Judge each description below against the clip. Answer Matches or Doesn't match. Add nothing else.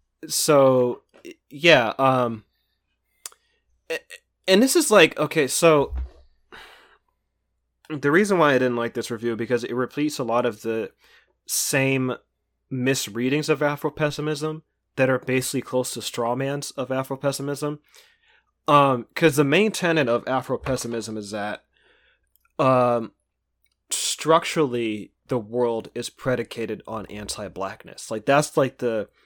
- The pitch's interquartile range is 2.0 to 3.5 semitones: Doesn't match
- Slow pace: Matches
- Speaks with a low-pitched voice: Matches